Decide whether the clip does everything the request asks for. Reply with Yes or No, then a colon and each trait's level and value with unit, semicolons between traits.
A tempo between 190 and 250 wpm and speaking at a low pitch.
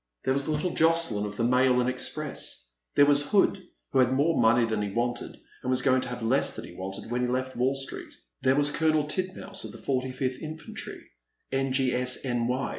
Yes: average, 200 wpm; low, 130 Hz